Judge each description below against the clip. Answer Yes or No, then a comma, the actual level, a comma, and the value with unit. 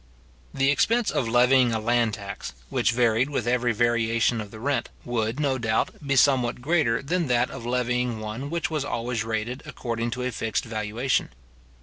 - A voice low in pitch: Yes, low, 120 Hz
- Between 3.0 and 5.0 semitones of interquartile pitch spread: No, narrow, 2.6 semitones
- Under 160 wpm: No, average, 180 wpm